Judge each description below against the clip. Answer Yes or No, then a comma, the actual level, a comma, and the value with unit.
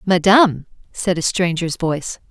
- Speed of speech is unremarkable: No, slow, 130 wpm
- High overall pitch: No, medium, 175 Hz